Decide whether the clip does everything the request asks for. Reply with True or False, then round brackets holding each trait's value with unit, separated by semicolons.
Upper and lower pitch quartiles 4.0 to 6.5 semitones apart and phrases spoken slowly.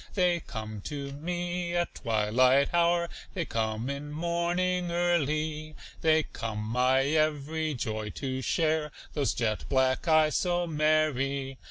True (4.6 semitones; 130 wpm)